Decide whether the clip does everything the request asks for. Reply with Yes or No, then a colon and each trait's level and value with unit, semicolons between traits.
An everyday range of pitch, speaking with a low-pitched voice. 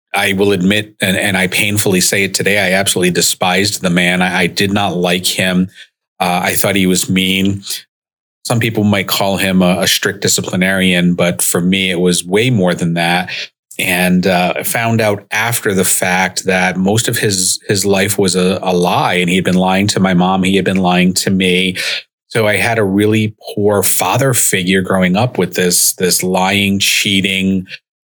No: narrow, 1.8 semitones; very low, 95 Hz